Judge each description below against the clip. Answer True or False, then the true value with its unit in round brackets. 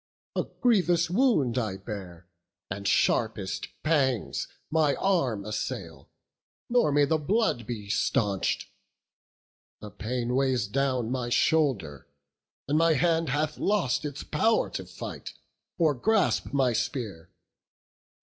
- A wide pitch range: True (6.9 semitones)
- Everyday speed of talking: False (120 wpm)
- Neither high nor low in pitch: False (130 Hz)